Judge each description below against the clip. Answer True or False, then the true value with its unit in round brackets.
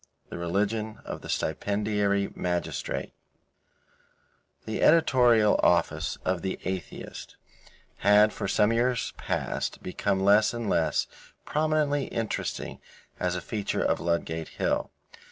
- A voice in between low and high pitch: False (105 Hz)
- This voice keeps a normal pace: False (115 wpm)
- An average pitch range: True (3.5 semitones)